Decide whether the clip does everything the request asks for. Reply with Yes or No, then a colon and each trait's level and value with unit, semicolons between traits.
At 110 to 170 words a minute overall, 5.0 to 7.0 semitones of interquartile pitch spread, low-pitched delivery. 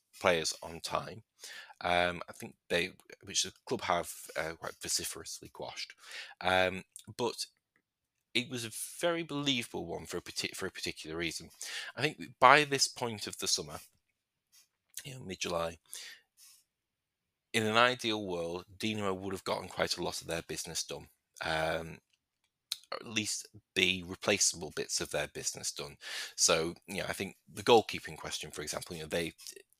Yes: average, 160 wpm; wide, 5.4 semitones; low, 105 Hz